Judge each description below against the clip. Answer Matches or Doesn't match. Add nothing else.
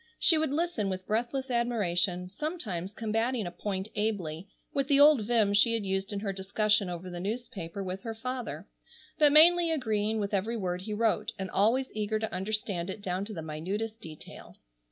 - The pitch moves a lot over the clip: Doesn't match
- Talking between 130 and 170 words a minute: Doesn't match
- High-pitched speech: Matches